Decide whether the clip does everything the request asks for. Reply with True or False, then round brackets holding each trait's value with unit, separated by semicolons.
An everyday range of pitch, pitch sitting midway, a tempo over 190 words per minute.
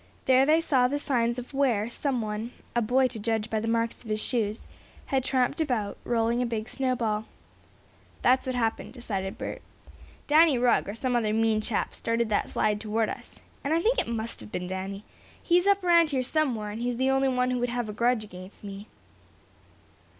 False (3.3 semitones; 235 Hz; 200 wpm)